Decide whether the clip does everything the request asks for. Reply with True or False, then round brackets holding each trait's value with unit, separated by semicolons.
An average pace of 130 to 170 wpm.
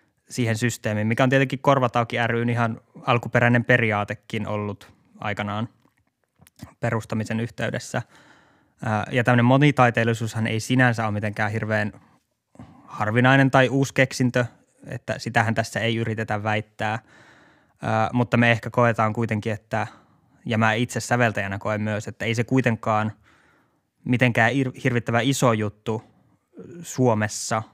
False (115 wpm)